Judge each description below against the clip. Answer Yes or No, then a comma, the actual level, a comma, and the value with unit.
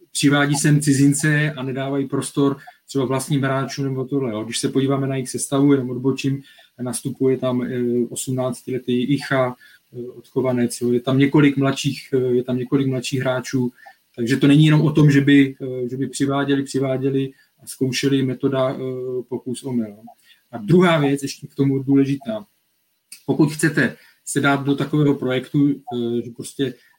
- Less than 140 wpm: No, average, 150 wpm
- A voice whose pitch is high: No, low, 135 Hz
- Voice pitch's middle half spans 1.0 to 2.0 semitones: Yes, narrow, 1.6 semitones